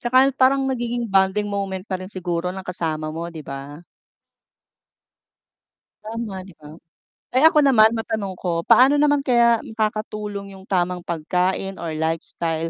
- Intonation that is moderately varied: Yes, average, 5.0 semitones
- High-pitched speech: Yes, high, 195 Hz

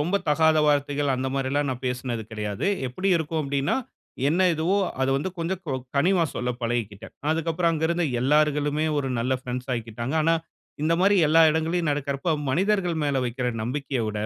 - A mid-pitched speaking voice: Yes, medium, 145 Hz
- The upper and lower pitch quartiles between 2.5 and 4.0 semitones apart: No, average, 4.4 semitones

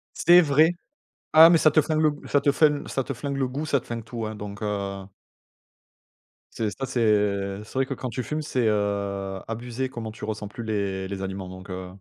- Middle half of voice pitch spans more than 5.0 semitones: Yes, wide, 5.6 semitones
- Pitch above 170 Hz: No, low, 115 Hz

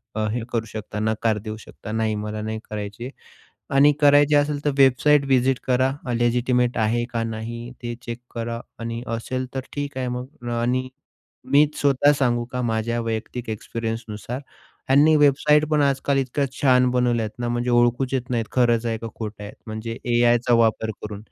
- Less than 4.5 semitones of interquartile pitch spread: Yes, average, 2.7 semitones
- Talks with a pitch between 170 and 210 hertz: No, low, 120 Hz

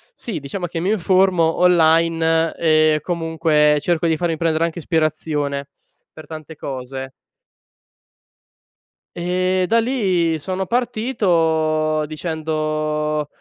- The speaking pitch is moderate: Yes, medium, 160 Hz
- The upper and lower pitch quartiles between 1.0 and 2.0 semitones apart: No, narrow, 2.4 semitones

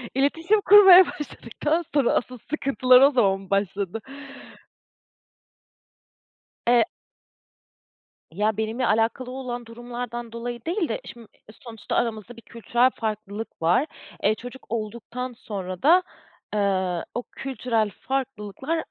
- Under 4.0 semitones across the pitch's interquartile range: Yes, average, 3.6 semitones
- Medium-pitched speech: No, high, 235 Hz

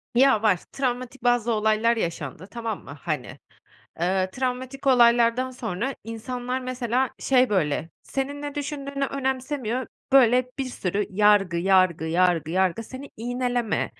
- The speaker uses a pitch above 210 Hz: Yes, high, 235 Hz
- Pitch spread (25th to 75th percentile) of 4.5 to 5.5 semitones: Yes, average, 5.1 semitones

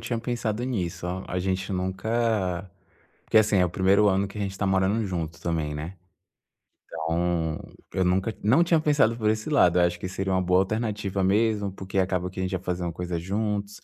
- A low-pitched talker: Yes, very low, 95 Hz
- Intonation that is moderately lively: Yes, average, 3.1 semitones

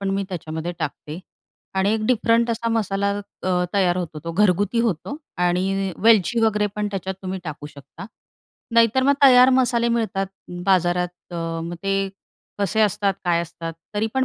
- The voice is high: Yes, high, 195 Hz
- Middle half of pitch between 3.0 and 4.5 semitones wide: Yes, average, 4.1 semitones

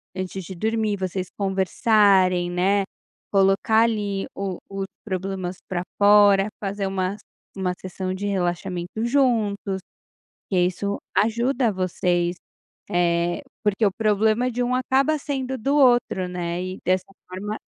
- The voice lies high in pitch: Yes, high, 195 Hz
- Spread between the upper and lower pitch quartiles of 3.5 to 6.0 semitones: No, average, 3.0 semitones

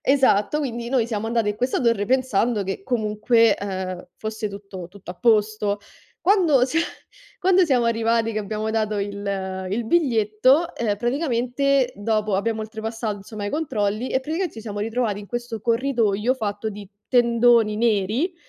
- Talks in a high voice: Yes, high, 225 Hz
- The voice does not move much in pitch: No, average, 3.2 semitones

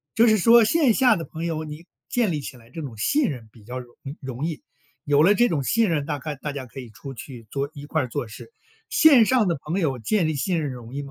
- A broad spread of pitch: Yes, wide, 7.1 semitones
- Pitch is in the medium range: Yes, medium, 150 Hz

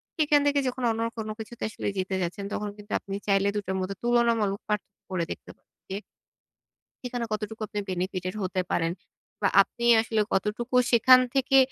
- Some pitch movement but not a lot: Yes, average, 3.6 semitones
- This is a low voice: No, high, 210 Hz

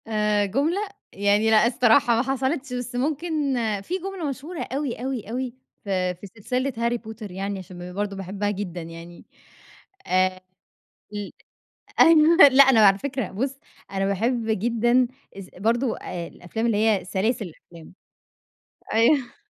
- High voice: Yes, high, 225 Hz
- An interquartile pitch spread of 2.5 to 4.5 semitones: No, average, 5.1 semitones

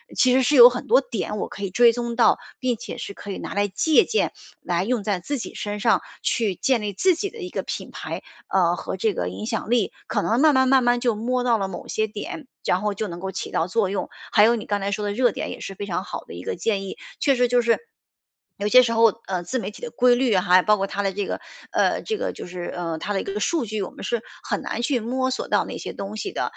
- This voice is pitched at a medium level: No, high, 215 Hz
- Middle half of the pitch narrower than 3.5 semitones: No, average, 4.2 semitones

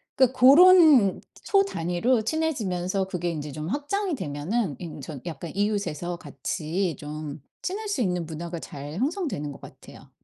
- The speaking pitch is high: No, medium, 180 Hz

